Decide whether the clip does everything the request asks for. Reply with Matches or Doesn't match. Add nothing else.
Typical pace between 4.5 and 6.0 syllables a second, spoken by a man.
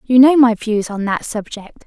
Doesn't match